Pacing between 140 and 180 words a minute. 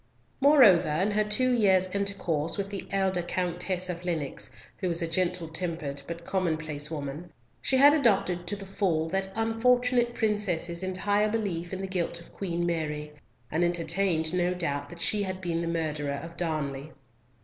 Yes: average, 170 wpm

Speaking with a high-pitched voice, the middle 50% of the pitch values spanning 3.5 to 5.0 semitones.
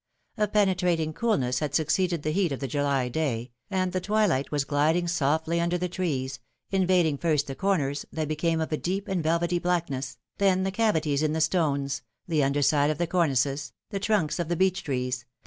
No: medium, 160 Hz; average, 4.2 semitones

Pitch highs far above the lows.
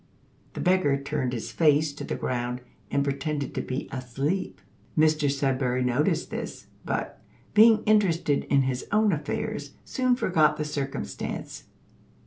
No: average, 3.4 semitones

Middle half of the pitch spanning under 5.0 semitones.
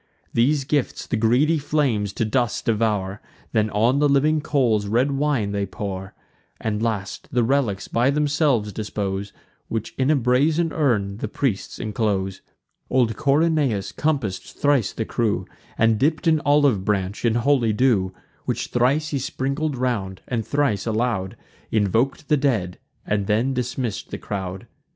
No: average, 5.3 semitones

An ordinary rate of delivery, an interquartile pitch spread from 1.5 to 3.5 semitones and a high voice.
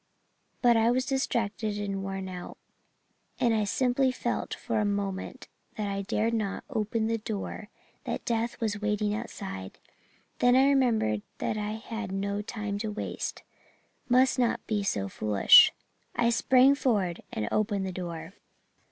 Yes: average, 150 wpm; average, 3.1 semitones; high, 215 Hz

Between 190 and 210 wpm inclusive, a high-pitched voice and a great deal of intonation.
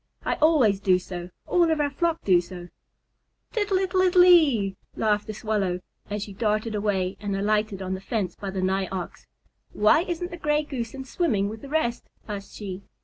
Yes: average, 195 wpm; high, 215 Hz; wide, 7.7 semitones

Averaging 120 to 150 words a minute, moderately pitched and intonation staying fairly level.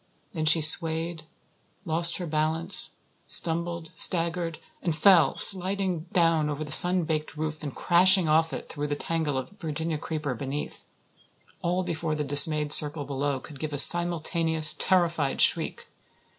Yes: average, 145 wpm; medium, 160 Hz; narrow, 2.1 semitones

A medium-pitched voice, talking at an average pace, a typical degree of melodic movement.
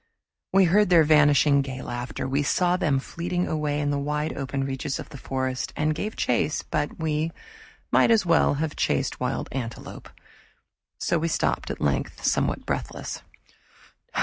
Yes: medium, 150 Hz; average, 160 wpm; average, 3.3 semitones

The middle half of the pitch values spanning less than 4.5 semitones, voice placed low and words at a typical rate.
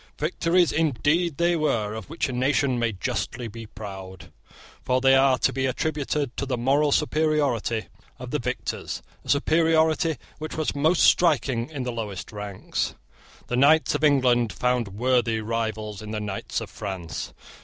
No: average, 5.3 semitones; low, 130 Hz; average, 160 wpm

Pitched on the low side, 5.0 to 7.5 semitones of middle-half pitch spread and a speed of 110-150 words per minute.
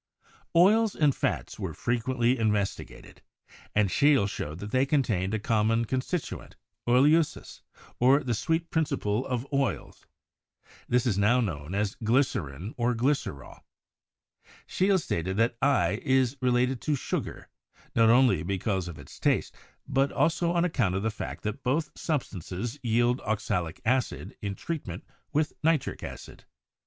Yes: low, 120 Hz; average, 5.3 semitones; average, 140 wpm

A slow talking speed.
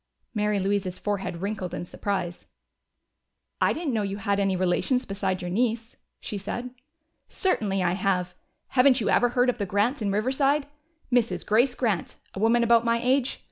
No: average, 170 wpm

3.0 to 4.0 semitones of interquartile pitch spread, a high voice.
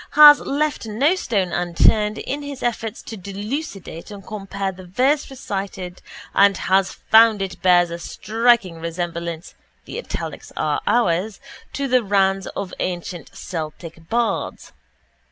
No: average, 4.7 semitones; high, 200 Hz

